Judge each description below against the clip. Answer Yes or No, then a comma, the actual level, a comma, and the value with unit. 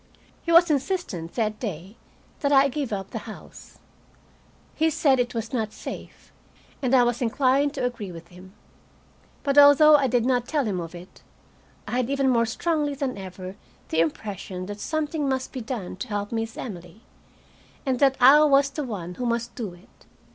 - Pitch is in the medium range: No, high, 245 Hz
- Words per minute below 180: No, average, 185 wpm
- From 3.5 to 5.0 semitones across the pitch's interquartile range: No, wide, 5.5 semitones